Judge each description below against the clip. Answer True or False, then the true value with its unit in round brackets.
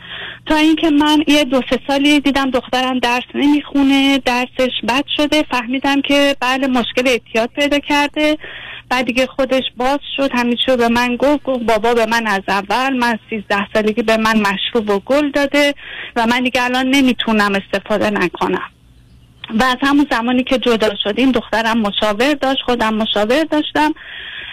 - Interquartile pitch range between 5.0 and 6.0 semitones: False (3.7 semitones)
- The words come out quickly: True (160 wpm)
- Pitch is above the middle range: True (255 Hz)